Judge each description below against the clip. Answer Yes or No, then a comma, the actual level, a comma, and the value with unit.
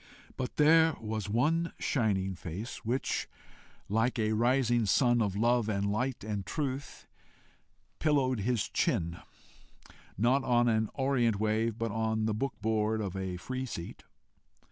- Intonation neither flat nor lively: Yes, average, 3.4 semitones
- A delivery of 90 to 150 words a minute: Yes, average, 140 wpm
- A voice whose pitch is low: Yes, low, 115 Hz